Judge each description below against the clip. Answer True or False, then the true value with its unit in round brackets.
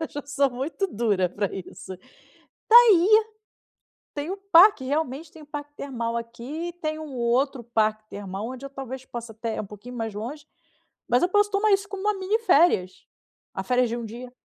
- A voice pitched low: False (265 Hz)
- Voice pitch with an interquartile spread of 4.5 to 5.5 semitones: False (6.1 semitones)